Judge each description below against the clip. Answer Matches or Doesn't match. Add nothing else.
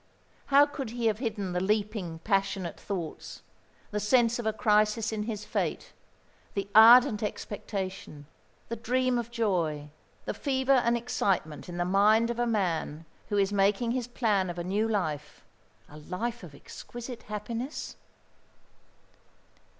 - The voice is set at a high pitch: Matches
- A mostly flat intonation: Doesn't match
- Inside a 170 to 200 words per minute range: Doesn't match